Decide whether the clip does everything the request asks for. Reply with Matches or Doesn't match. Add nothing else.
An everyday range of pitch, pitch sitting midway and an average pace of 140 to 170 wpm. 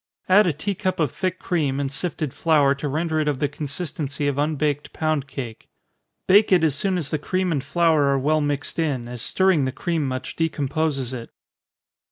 Doesn't match